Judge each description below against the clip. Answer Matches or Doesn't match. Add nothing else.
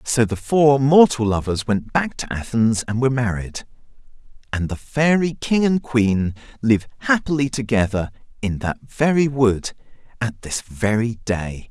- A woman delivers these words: Doesn't match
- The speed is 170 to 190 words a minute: Doesn't match